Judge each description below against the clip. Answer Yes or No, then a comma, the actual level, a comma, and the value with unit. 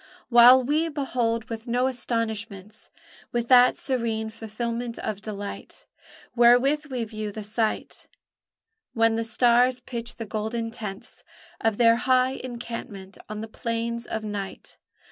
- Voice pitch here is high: Yes, high, 230 Hz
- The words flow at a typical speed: No, slow, 130 wpm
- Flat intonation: Yes, narrow, 2.0 semitones